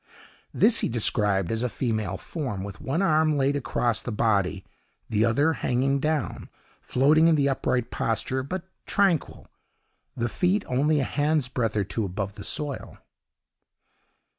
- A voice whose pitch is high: No, low, 130 Hz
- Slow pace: No, average, 150 wpm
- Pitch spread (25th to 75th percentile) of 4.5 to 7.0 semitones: Yes, wide, 5.6 semitones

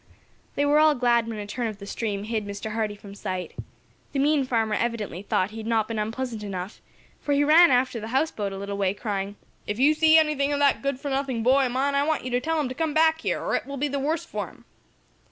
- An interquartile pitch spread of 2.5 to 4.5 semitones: No, average, 5.2 semitones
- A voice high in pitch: Yes, high, 245 Hz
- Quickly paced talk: Yes, fast, 260 wpm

